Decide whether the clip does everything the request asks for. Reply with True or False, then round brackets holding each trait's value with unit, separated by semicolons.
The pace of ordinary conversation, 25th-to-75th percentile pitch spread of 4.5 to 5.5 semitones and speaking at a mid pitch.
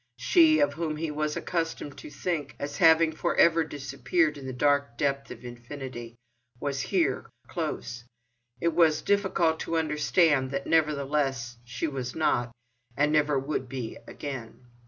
False (150 wpm; 3.5 semitones; 145 Hz)